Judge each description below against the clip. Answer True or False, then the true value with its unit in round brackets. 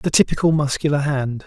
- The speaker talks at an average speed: True (165 wpm)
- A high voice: False (140 Hz)